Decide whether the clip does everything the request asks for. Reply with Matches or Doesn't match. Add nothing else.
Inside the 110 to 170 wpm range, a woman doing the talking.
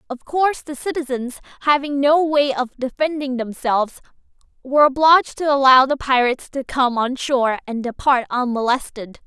Matches